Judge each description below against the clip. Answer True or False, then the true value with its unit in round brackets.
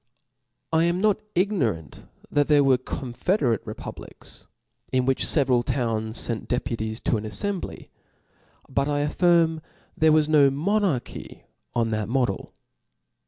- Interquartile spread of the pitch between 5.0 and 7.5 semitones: True (5.5 semitones)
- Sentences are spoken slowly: True (130 wpm)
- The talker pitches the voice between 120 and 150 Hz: True (135 Hz)